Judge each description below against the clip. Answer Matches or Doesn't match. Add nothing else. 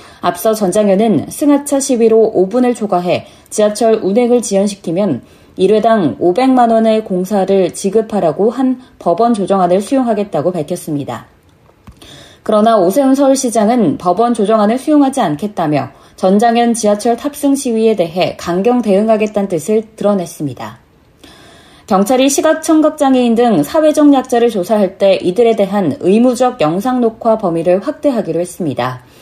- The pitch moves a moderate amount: Matches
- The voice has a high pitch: Matches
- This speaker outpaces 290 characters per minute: Matches